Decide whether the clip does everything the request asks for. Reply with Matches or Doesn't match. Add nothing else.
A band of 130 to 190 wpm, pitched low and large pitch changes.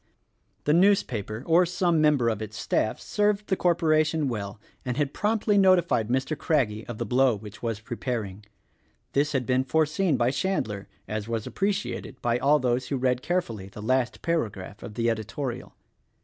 Matches